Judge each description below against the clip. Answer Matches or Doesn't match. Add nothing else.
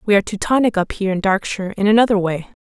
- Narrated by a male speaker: Doesn't match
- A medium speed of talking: Doesn't match